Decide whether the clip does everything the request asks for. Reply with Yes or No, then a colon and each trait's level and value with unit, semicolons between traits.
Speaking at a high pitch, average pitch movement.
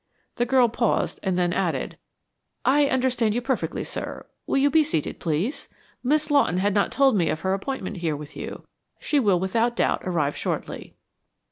No: high, 225 Hz; wide, 6.6 semitones